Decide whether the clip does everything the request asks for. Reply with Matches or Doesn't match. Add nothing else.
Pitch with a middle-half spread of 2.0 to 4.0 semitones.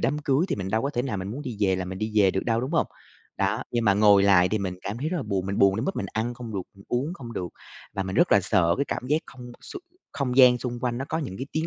Doesn't match